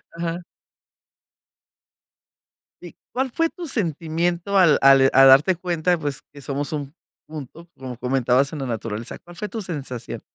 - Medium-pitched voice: Yes, medium, 150 Hz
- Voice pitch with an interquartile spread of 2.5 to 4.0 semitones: No, average, 4.7 semitones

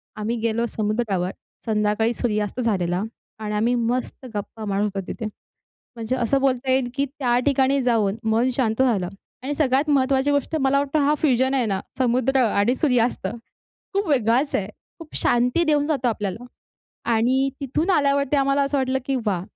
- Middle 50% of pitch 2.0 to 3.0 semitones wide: No, average, 3.9 semitones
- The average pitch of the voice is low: No, high, 245 Hz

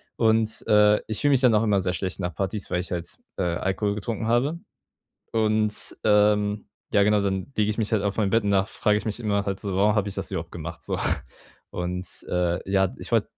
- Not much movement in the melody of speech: Yes, narrow, 2.1 semitones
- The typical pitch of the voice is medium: No, low, 105 Hz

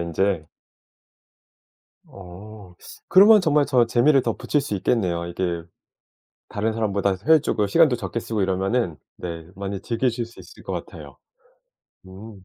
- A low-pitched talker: Yes, low, 105 Hz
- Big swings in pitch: No, average, 4.4 semitones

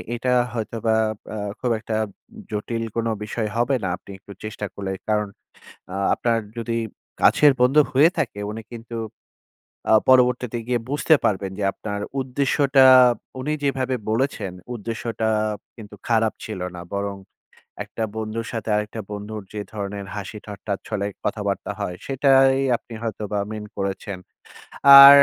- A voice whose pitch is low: Yes, low, 110 Hz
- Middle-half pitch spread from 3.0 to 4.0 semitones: Yes, average, 3.4 semitones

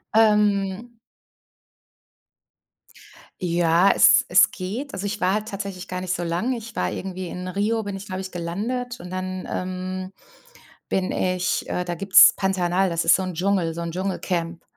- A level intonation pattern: Yes, narrow, 2.0 semitones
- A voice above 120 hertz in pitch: Yes, medium, 185 Hz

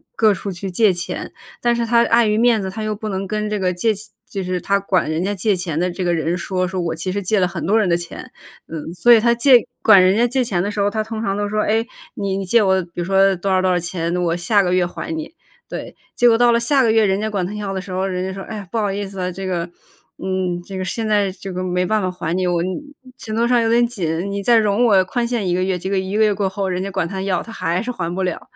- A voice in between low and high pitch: No, high, 195 Hz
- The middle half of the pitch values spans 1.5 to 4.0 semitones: Yes, average, 3.0 semitones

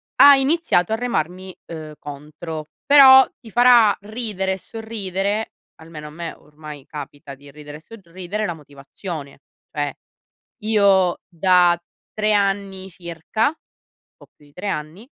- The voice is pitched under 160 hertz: No, medium, 185 Hz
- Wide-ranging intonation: Yes, wide, 5.8 semitones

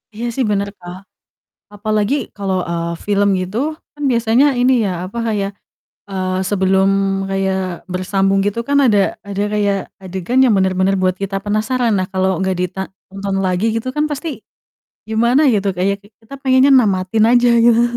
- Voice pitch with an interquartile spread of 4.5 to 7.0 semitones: No, average, 3.3 semitones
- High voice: Yes, high, 200 Hz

